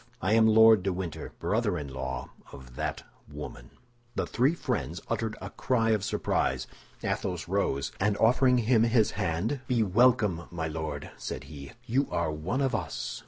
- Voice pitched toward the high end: No, low, 100 Hz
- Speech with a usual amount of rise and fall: No, wide, 6.3 semitones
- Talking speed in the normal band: Yes, average, 165 wpm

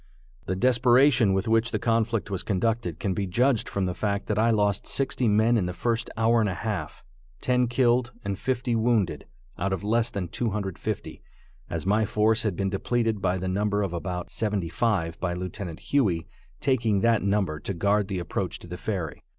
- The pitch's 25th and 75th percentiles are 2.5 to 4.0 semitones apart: Yes, average, 3.6 semitones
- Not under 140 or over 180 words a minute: No, average, 190 wpm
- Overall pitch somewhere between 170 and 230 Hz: No, low, 105 Hz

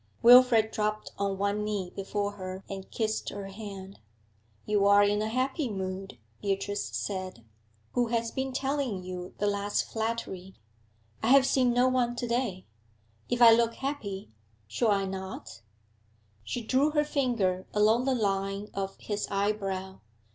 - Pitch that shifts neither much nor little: Yes, average, 3.7 semitones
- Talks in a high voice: Yes, high, 210 Hz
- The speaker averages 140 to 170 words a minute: Yes, average, 150 wpm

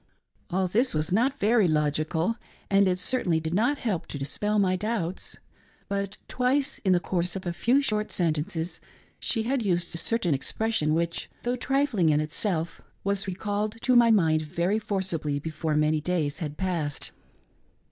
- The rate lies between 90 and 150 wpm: No, average, 165 wpm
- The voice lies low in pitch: No, medium, 185 Hz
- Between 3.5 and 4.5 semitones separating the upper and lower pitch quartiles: No, average, 5.3 semitones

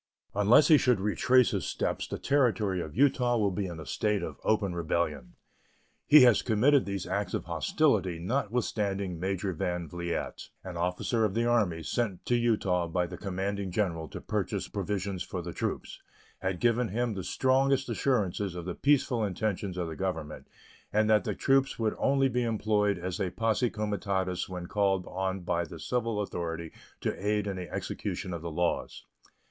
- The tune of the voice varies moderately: Yes, average, 4.4 semitones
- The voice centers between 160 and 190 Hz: No, low, 100 Hz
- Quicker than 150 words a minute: Yes, average, 175 wpm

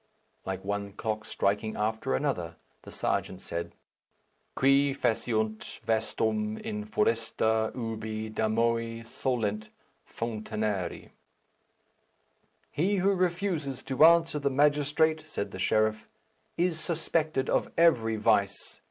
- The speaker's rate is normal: No, slow, 105 wpm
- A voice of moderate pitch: No, low, 115 Hz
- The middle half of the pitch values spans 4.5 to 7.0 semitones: Yes, average, 5.2 semitones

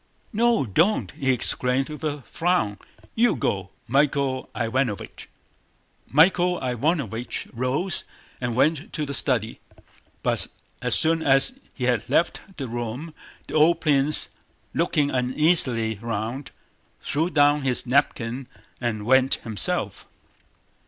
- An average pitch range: Yes, average, 4.4 semitones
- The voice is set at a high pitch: No, low, 135 Hz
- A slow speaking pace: Yes, slow, 120 wpm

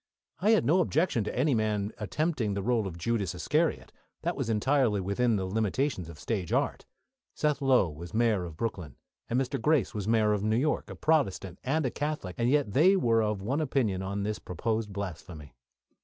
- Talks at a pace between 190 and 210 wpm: Yes, average, 195 wpm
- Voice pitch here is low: Yes, low, 110 Hz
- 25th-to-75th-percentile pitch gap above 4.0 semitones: Yes, wide, 5.6 semitones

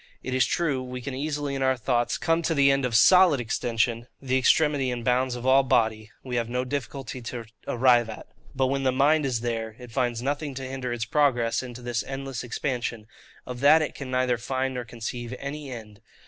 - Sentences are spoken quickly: Yes, fast, 210 wpm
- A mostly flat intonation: Yes, narrow, 2.3 semitones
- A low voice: Yes, low, 130 Hz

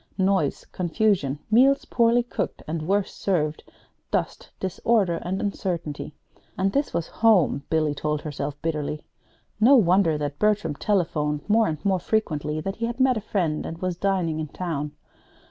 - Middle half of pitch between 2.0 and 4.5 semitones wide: No, wide, 5.5 semitones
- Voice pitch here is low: No, medium, 175 Hz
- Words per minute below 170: Yes, average, 155 wpm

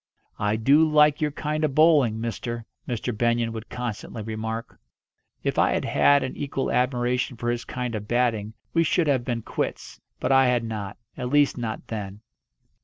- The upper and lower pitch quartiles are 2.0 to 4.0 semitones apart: Yes, average, 3.6 semitones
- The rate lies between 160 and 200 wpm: Yes, average, 180 wpm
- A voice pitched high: No, low, 120 Hz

